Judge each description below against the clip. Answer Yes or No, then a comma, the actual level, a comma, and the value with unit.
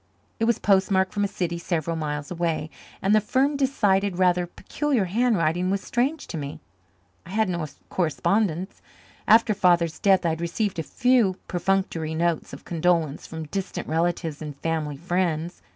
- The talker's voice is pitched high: No, medium, 180 Hz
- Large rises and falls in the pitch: No, average, 3.7 semitones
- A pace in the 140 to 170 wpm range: Yes, average, 160 wpm